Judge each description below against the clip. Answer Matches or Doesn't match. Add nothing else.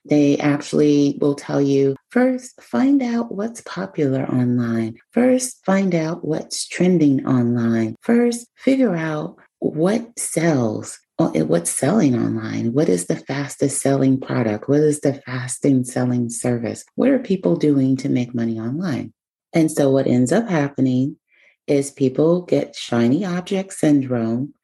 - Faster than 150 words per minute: Doesn't match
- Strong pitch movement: Matches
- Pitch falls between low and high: Matches